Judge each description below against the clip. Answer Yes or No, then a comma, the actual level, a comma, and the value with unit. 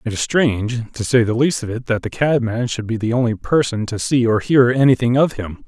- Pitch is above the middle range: No, low, 120 Hz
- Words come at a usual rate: No, fast, 255 wpm